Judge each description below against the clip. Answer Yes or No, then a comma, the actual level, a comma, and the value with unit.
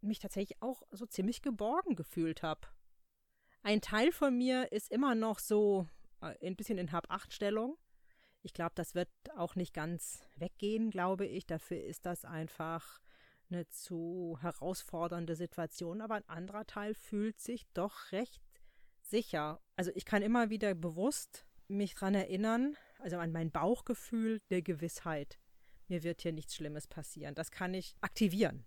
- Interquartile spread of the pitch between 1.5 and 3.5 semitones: No, average, 4.2 semitones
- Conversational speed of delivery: Yes, average, 155 wpm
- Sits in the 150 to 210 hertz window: Yes, high, 190 Hz